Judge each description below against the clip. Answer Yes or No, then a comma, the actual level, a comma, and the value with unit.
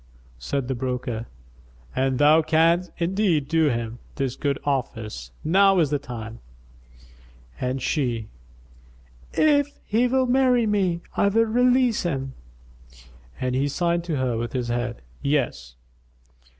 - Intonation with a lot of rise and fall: Yes, wide, 7.4 semitones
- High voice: No, medium, 145 Hz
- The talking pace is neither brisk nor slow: No, slow, 130 wpm